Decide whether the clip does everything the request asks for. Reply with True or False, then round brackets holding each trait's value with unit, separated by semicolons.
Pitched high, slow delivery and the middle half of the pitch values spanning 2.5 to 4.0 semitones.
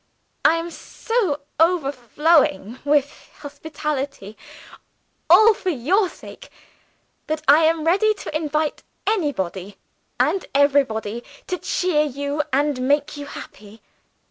True (295 Hz; 110 wpm; 3.5 semitones)